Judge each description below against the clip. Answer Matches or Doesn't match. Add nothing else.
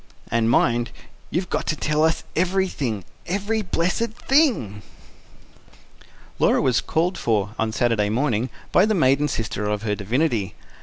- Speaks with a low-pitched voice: Matches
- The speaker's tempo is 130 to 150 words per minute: Matches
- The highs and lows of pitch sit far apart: Matches